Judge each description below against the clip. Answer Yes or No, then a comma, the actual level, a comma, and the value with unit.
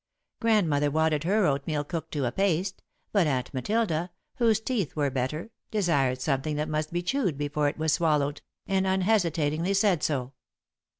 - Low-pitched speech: No, medium, 160 Hz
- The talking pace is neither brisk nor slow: Yes, average, 160 wpm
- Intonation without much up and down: No, average, 4.8 semitones